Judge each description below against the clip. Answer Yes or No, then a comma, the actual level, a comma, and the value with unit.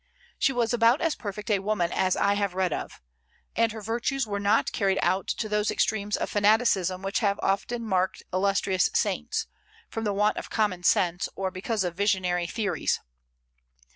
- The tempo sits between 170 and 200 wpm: Yes, average, 175 wpm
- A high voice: Yes, high, 205 Hz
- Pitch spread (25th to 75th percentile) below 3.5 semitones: Yes, average, 2.8 semitones